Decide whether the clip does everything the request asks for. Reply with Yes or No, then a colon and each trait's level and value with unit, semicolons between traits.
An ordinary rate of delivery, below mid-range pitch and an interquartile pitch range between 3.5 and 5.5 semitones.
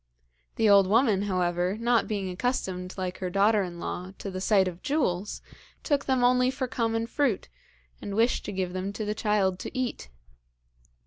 No: average, 180 wpm; high, 205 Hz; average, 3.9 semitones